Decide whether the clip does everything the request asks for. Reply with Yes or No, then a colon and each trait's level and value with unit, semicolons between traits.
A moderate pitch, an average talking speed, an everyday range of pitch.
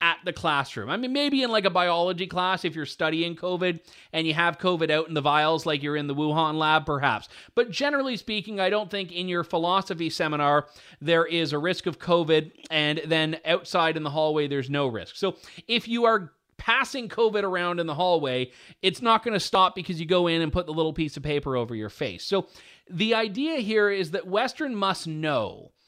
No: medium, 170 Hz; fast, 215 wpm; average, 3.8 semitones